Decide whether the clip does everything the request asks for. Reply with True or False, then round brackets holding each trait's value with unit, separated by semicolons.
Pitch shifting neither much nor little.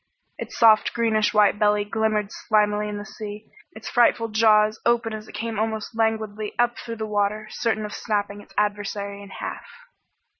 False (1.1 semitones)